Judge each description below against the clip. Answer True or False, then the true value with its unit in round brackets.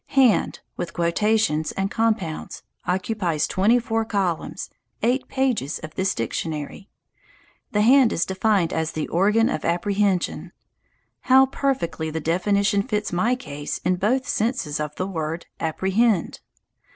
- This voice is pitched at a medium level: False (195 Hz)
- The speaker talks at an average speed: False (130 wpm)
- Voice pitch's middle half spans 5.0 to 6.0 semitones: True (5.4 semitones)